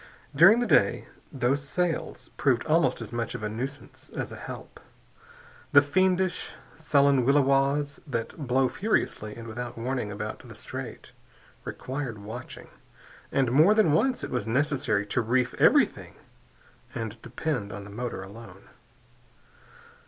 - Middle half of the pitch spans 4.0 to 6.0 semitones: Yes, average, 4.3 semitones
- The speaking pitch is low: Yes, low, 130 Hz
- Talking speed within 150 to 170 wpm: No, slow, 135 wpm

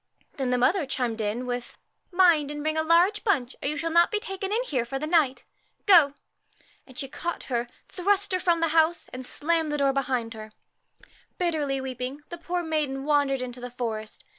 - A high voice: Yes, very high, 290 Hz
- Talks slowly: No, fast, 205 wpm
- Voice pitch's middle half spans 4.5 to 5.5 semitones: Yes, average, 5.2 semitones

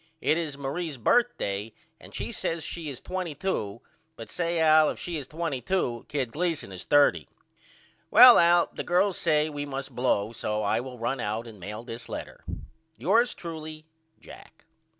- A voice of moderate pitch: Yes, medium, 145 Hz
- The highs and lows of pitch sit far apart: Yes, wide, 6.3 semitones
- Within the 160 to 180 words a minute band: Yes, average, 165 wpm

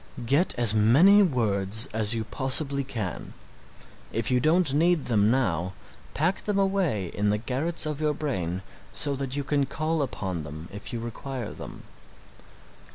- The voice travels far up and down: Yes, wide, 6.4 semitones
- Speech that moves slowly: No, average, 160 wpm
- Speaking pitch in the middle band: No, low, 130 Hz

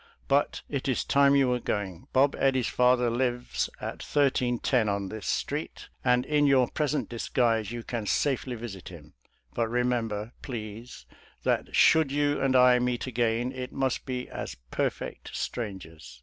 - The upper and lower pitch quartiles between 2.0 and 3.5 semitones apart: Yes, average, 2.8 semitones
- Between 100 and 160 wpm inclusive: Yes, average, 155 wpm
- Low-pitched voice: Yes, low, 125 Hz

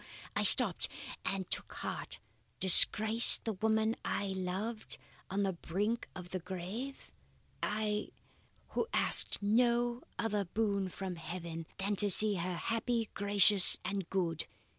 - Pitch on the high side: Yes, high, 200 Hz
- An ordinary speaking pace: No, slow, 130 wpm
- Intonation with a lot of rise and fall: No, average, 3.0 semitones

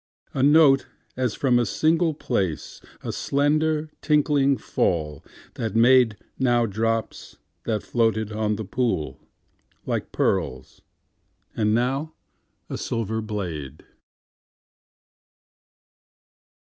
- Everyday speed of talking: No, slow, 85 wpm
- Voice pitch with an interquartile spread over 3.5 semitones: Yes, average, 4.7 semitones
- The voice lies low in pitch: Yes, low, 120 Hz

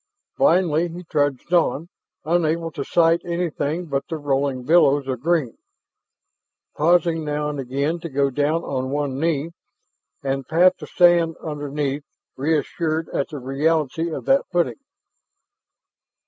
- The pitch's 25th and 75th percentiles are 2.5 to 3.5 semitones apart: Yes, average, 3.2 semitones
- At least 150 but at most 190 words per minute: No, slow, 135 wpm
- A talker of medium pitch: Yes, medium, 155 Hz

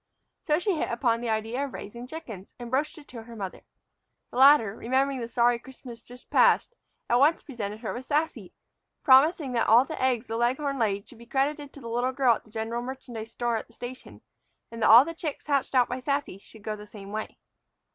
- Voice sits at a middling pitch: No, high, 245 Hz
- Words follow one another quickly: Yes, fast, 220 wpm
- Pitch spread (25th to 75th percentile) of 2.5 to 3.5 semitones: Yes, average, 3.2 semitones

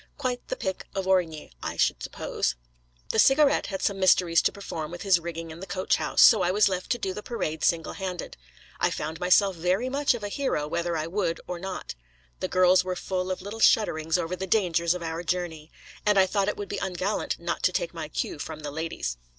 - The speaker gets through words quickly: Yes, fast, 225 wpm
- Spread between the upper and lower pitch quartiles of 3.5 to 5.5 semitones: No, average, 3.1 semitones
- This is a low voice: No, medium, 185 Hz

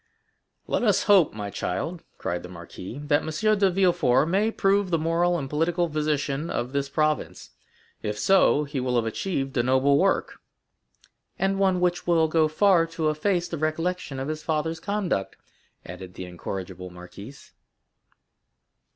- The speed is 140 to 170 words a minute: Yes, average, 155 wpm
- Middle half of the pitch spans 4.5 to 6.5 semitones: Yes, average, 5.2 semitones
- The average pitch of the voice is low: No, medium, 155 Hz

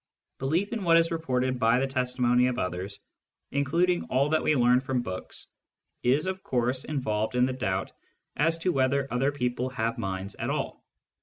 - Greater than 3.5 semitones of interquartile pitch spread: No, average, 3.2 semitones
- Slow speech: No, average, 175 wpm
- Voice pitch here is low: Yes, low, 130 Hz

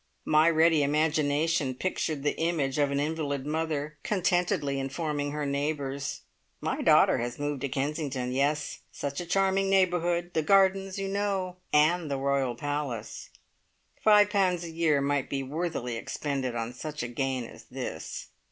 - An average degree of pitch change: Yes, average, 3.7 semitones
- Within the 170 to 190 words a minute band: No, average, 150 wpm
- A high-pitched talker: No, medium, 150 Hz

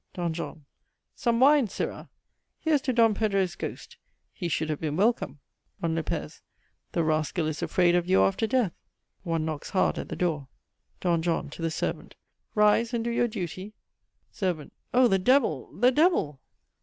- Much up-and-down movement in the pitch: Yes, wide, 6.2 semitones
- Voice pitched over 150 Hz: Yes, medium, 185 Hz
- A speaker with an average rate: Yes, average, 170 wpm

